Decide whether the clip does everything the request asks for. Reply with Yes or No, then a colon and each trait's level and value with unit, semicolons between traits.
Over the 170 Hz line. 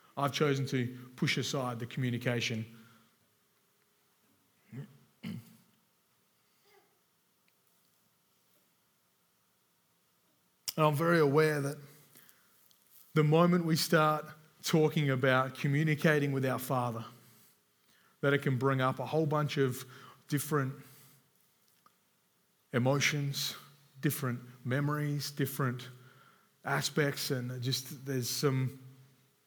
No: medium, 140 Hz